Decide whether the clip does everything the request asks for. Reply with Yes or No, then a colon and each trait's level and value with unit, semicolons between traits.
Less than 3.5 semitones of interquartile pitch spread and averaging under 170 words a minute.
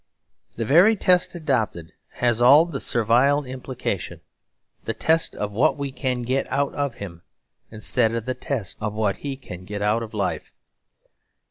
No: average, 4.7 semitones; average, 160 wpm